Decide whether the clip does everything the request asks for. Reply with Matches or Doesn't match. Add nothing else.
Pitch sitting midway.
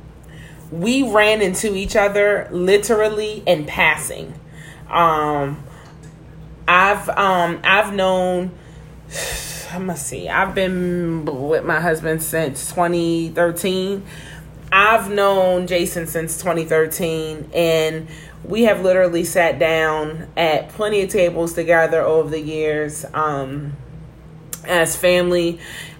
Matches